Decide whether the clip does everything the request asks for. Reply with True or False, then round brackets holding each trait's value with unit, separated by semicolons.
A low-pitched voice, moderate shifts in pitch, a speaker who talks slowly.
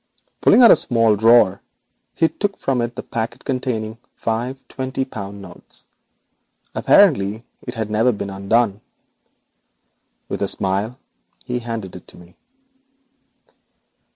True (115 Hz; 3.8 semitones; 130 wpm)